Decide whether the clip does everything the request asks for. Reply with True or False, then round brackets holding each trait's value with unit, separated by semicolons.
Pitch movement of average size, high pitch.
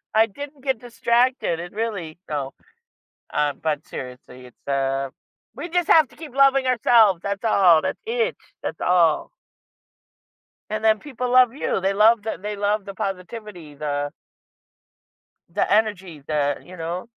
False (6.9 semitones; 205 Hz)